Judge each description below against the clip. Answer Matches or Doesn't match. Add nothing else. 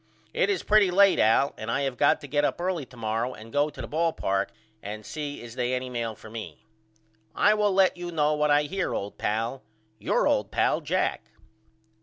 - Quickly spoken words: Matches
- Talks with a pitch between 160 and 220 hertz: Doesn't match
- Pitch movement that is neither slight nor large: Doesn't match